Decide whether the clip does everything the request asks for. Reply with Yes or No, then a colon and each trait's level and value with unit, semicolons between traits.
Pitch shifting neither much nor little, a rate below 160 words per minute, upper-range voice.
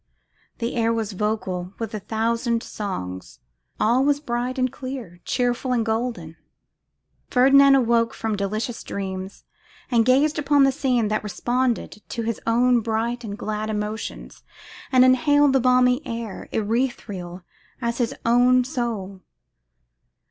Yes: average, 3.0 semitones; slow, 135 wpm; high, 235 Hz